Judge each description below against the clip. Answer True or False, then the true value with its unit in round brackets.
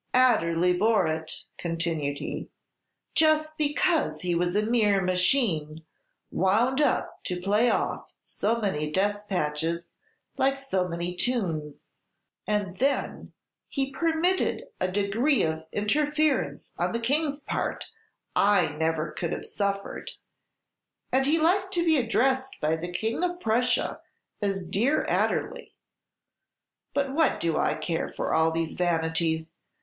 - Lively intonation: True (8.3 semitones)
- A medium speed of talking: False (130 wpm)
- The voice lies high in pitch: True (205 Hz)